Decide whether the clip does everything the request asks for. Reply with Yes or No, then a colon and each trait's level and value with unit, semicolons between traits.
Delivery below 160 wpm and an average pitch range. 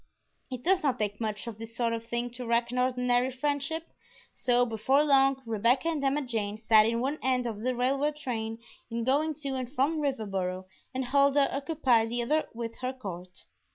No: average, 190 wpm; average, 3.3 semitones